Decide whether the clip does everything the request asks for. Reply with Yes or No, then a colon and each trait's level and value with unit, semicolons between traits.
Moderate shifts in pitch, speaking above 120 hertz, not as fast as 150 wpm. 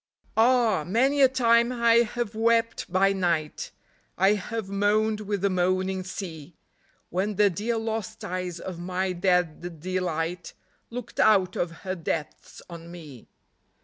Yes: average, 4.0 semitones; high, 190 Hz; average, 140 wpm